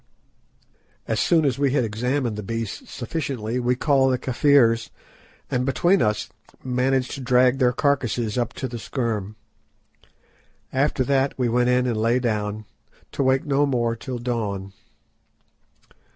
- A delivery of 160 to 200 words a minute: No, average, 145 wpm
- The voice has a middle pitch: No, low, 125 Hz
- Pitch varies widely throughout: No, average, 2.7 semitones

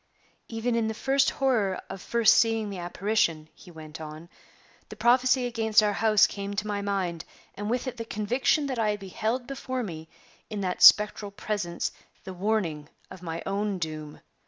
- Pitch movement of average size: Yes, average, 4.2 semitones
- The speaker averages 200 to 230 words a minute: No, average, 175 wpm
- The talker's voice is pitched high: Yes, high, 210 Hz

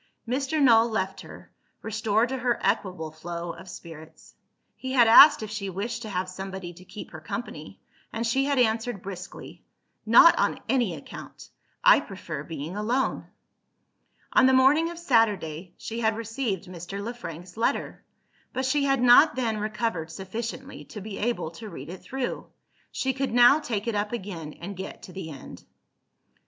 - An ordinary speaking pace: Yes, average, 170 wpm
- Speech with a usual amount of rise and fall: Yes, average, 4.9 semitones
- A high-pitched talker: Yes, high, 220 Hz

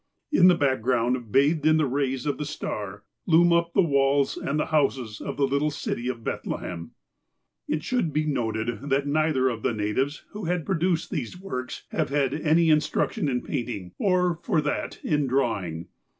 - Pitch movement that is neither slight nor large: Yes, average, 4.3 semitones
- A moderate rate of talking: Yes, average, 180 wpm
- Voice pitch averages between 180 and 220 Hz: No, medium, 140 Hz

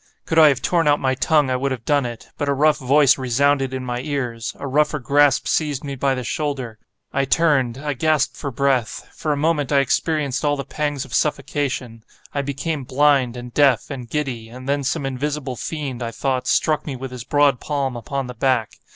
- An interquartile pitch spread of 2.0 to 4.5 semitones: Yes, narrow, 2.4 semitones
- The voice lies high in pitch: No, medium, 140 Hz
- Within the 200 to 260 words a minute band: Yes, fast, 205 wpm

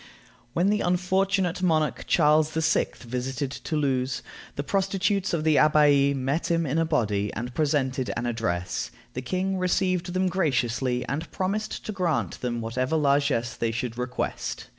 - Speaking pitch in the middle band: Yes, medium, 150 Hz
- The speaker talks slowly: No, average, 150 wpm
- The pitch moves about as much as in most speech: No, wide, 6.0 semitones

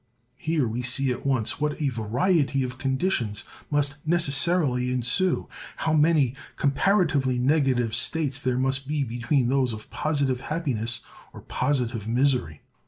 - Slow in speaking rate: Yes, slow, 130 wpm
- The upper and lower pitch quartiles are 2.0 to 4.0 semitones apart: Yes, average, 3.3 semitones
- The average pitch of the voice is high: No, low, 135 Hz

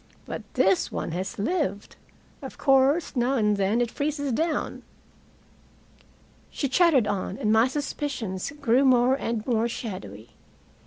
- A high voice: Yes, high, 240 Hz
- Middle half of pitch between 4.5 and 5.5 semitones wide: Yes, average, 5.2 semitones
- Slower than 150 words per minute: Yes, slow, 135 wpm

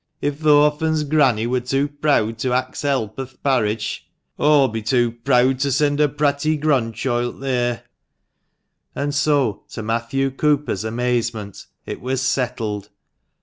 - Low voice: Yes, low, 130 Hz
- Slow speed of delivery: No, average, 145 wpm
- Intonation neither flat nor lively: Yes, average, 3.6 semitones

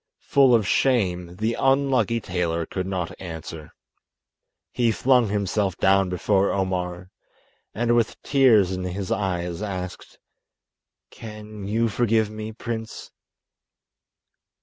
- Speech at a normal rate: No, slow, 110 wpm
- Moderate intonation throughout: Yes, average, 3.9 semitones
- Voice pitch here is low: Yes, low, 100 Hz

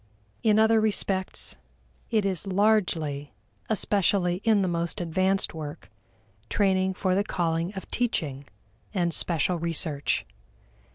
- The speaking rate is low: Yes, slow, 115 wpm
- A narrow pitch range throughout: No, average, 3.4 semitones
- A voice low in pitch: No, medium, 185 Hz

